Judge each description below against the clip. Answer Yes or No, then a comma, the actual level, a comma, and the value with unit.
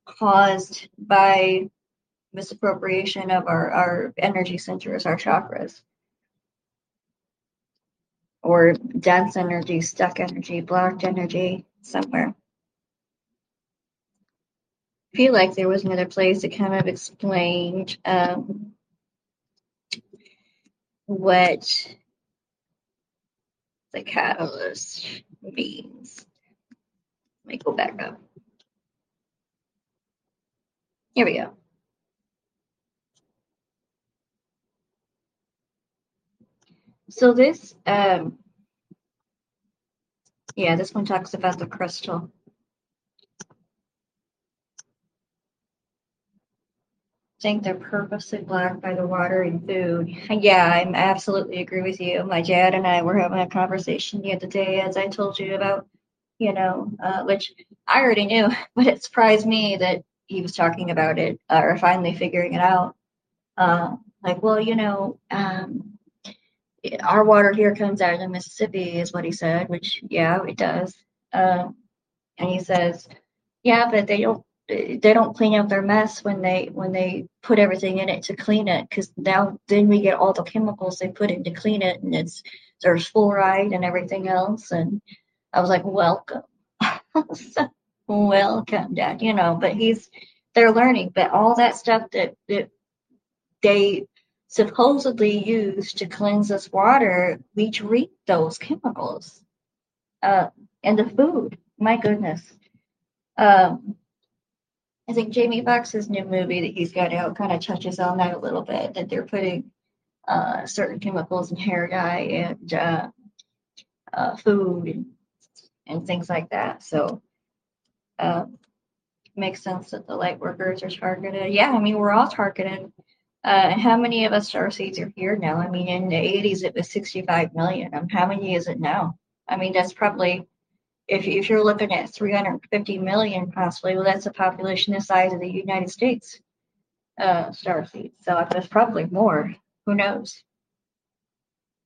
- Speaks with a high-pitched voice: Yes, high, 195 Hz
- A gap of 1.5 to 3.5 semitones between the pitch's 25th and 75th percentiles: Yes, narrow, 2.5 semitones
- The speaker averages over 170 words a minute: No, slow, 135 wpm